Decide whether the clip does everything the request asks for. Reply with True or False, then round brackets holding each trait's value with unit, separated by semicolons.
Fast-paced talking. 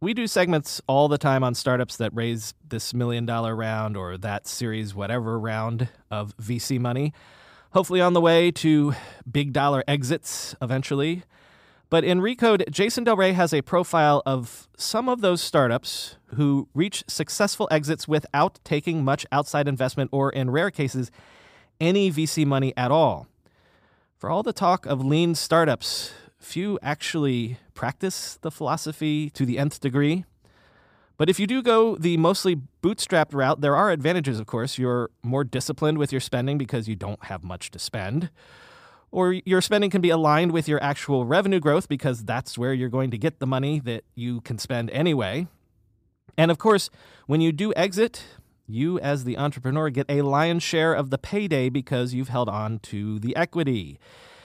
False (170 wpm)